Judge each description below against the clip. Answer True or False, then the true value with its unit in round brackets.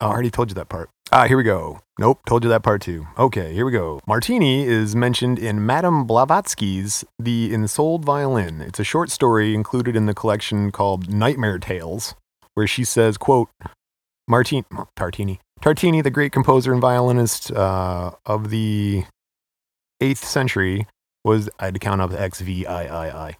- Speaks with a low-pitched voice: True (110 Hz)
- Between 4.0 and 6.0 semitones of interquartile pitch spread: True (4.5 semitones)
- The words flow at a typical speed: True (175 wpm)